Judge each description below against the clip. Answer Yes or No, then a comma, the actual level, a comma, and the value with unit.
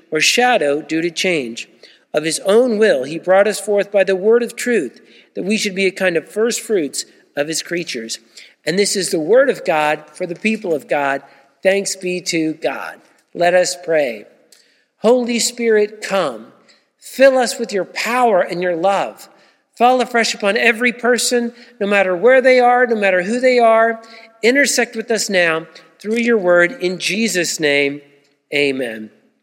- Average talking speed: Yes, average, 175 wpm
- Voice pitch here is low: No, high, 195 Hz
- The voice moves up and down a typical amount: No, wide, 6.0 semitones